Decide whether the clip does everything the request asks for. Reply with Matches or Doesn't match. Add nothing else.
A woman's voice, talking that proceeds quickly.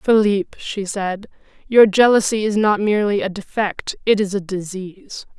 Doesn't match